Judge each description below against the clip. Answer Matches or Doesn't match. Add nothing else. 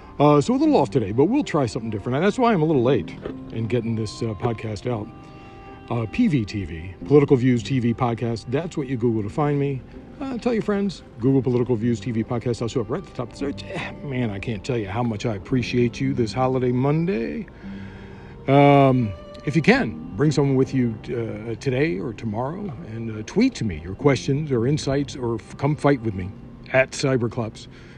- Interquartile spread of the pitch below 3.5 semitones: Doesn't match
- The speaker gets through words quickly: Matches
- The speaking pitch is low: Matches